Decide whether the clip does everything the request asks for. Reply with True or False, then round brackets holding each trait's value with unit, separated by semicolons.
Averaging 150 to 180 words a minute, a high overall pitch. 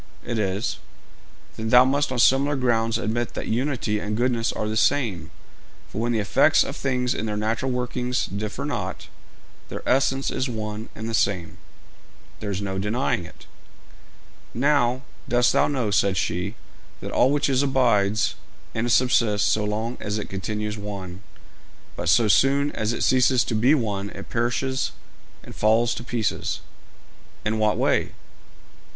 False (160 wpm; 115 Hz)